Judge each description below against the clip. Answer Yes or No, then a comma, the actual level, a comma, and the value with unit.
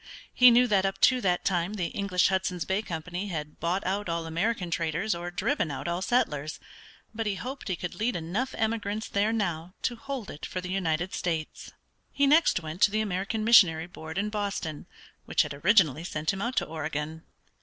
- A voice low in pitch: No, medium, 185 Hz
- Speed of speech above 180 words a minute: Yes, average, 195 wpm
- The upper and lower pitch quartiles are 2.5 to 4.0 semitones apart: No, average, 4.5 semitones